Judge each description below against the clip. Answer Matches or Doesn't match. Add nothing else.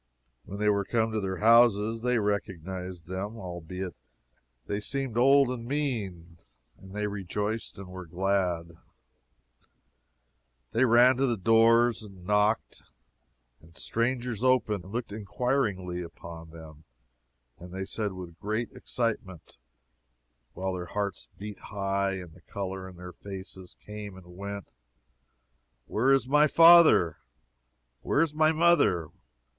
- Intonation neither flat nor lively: Matches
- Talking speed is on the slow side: Matches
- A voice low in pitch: Matches